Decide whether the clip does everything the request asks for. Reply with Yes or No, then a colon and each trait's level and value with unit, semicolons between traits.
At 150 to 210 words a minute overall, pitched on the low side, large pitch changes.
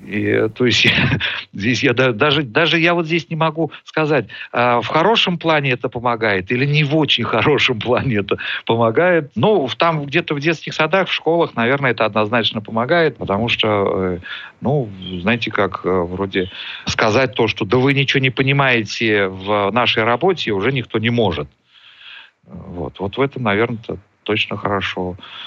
Yes: average, 155 wpm; low, 120 Hz; wide, 6.5 semitones